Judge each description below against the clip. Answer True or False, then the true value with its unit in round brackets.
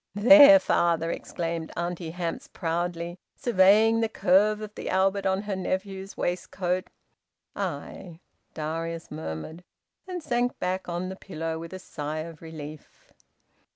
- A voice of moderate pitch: True (180 Hz)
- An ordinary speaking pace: False (130 wpm)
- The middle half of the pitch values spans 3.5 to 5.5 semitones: False (3.0 semitones)